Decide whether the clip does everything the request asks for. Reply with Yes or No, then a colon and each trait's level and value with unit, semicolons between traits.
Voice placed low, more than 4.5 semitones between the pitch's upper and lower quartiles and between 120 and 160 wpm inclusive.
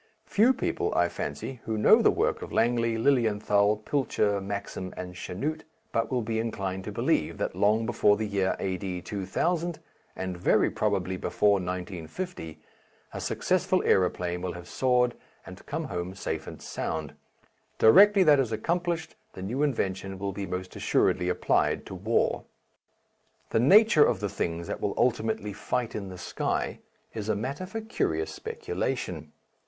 Yes: low, 105 Hz; wide, 5.5 semitones; average, 155 wpm